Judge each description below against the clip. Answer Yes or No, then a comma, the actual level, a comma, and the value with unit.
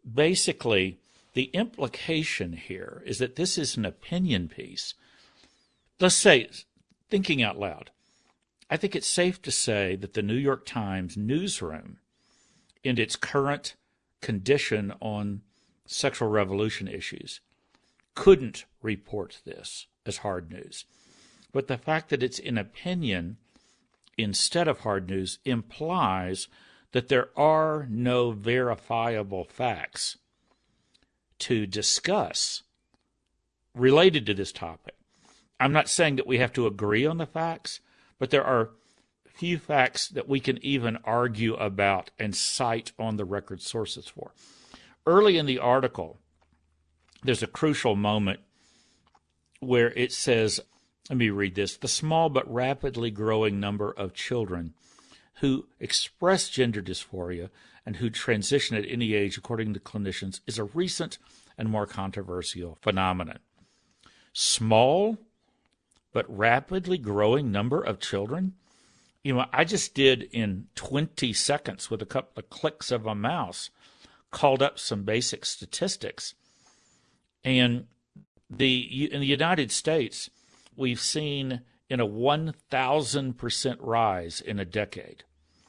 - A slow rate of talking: Yes, slow, 125 wpm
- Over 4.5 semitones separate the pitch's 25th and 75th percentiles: Yes, wide, 5.6 semitones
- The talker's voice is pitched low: Yes, low, 120 Hz